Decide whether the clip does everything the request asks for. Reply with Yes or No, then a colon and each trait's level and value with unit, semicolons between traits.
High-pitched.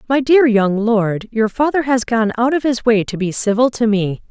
Yes: high, 230 Hz